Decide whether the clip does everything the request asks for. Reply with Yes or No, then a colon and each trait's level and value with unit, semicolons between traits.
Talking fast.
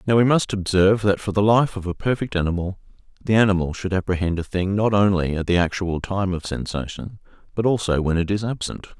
Yes: fast, 215 wpm